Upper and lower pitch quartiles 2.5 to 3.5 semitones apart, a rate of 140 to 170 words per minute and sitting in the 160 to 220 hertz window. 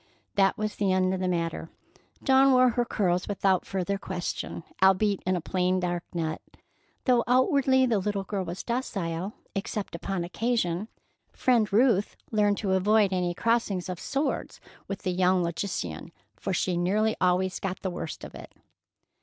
Yes: average, 3.2 semitones; average, 160 wpm; high, 190 Hz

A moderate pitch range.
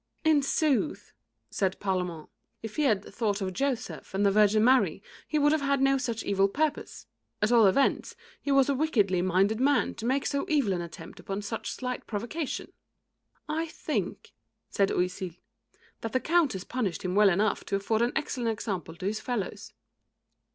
No: wide, 6.0 semitones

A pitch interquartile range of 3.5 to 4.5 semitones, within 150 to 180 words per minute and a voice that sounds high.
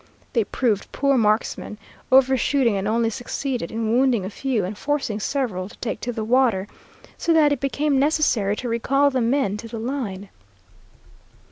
Yes: average, 4.2 semitones; average, 165 wpm; high, 240 Hz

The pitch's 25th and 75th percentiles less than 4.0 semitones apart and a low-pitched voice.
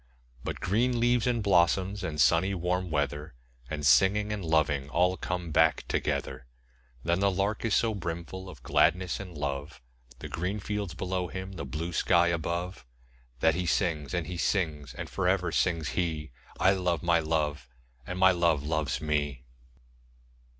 Yes: average, 3.4 semitones; very low, 85 Hz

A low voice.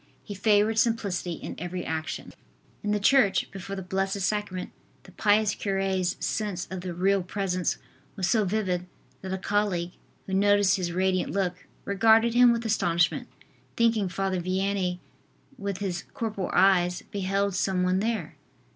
No: high, 195 Hz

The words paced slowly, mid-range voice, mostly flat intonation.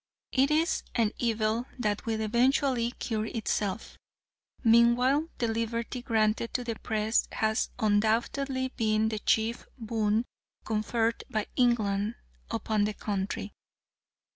No: slow, 115 wpm; high, 225 Hz; narrow, 2.0 semitones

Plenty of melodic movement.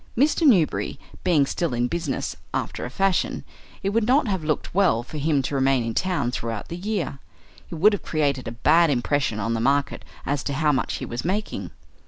Yes: wide, 6.3 semitones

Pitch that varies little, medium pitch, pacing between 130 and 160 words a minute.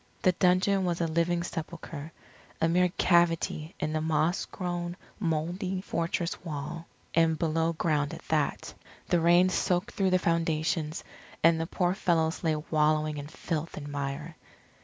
Yes: narrow, 2.1 semitones; medium, 165 Hz; average, 150 wpm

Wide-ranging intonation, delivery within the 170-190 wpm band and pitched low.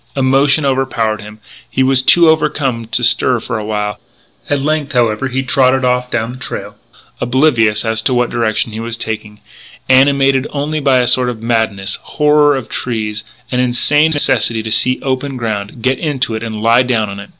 No: average, 3.3 semitones; average, 185 wpm; low, 125 Hz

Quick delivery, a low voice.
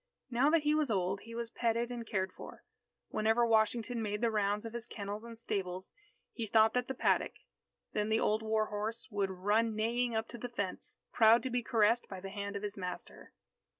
No: fast, 210 wpm; high, 220 Hz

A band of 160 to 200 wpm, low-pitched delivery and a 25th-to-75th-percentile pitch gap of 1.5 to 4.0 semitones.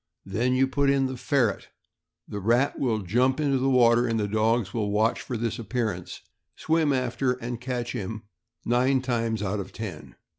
Yes: average, 180 wpm; low, 120 Hz; average, 3.0 semitones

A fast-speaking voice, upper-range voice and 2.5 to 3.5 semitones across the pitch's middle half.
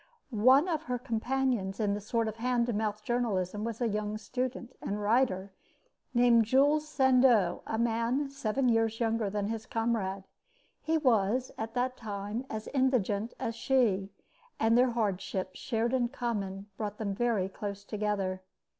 No: average, 155 wpm; high, 225 Hz; average, 3.2 semitones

